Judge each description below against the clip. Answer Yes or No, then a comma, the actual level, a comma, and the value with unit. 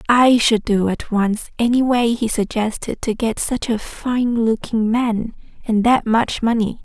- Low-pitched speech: No, high, 225 Hz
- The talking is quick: No, average, 175 wpm